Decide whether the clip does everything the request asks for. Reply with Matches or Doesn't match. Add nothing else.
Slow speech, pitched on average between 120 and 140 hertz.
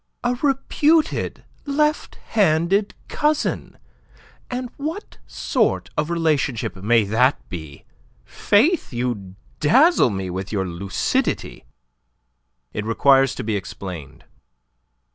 Matches